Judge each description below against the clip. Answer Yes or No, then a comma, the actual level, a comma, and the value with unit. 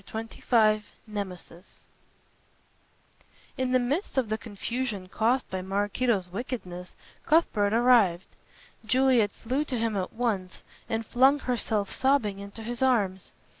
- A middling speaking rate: No, slow, 125 wpm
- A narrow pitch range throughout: No, average, 4.0 semitones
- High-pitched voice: Yes, high, 225 Hz